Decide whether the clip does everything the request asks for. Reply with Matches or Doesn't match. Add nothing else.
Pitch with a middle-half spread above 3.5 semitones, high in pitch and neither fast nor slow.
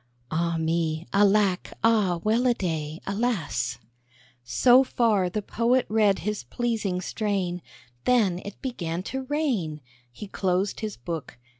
Doesn't match